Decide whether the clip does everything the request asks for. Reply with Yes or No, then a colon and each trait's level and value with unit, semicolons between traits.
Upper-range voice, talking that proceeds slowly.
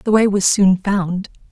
No: high, 195 Hz; average, 200 wpm